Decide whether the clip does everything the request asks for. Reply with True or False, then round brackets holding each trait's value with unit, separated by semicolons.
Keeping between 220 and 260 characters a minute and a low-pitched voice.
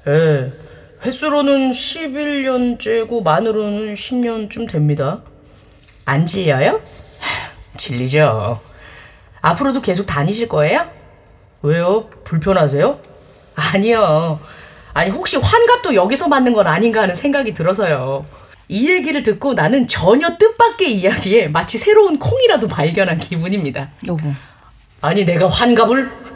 False (255 characters per minute; 190 Hz)